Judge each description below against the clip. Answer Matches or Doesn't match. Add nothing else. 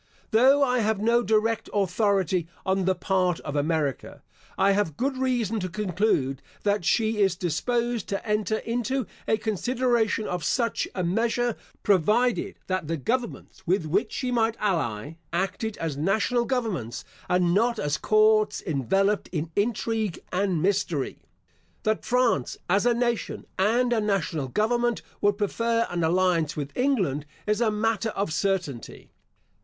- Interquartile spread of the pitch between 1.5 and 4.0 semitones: Doesn't match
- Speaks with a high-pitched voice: Matches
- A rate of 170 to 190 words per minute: Doesn't match